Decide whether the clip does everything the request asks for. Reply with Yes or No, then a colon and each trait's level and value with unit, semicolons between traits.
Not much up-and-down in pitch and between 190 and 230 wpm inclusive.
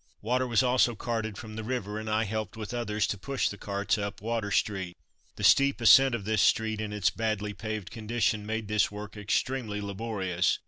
Yes: narrow, 1.9 semitones; average, 195 wpm